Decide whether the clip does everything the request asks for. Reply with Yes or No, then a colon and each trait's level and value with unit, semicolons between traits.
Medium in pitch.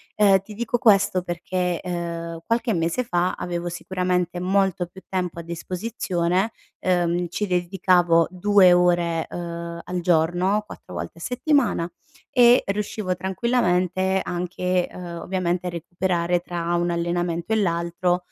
Yes: medium, 180 Hz